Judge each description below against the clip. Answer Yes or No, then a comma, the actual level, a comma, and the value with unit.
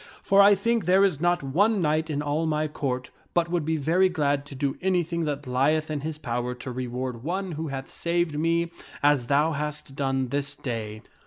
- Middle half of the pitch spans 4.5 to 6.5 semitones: No, average, 3.8 semitones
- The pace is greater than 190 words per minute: Yes, average, 200 wpm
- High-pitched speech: No, medium, 150 Hz